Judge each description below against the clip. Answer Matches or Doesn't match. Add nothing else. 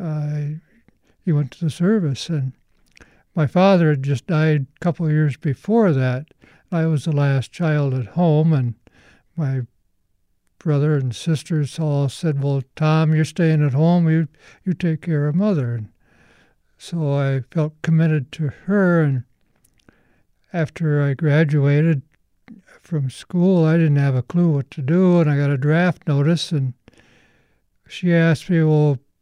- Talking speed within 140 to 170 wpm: Matches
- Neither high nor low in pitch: Matches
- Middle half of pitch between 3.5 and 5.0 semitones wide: Doesn't match